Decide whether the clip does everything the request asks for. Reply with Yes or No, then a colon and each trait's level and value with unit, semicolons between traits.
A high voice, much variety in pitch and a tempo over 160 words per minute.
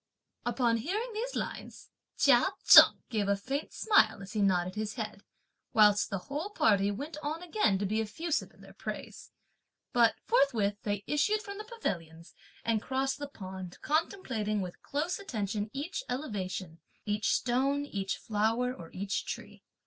No: high, 225 Hz; wide, 6.7 semitones; average, 155 wpm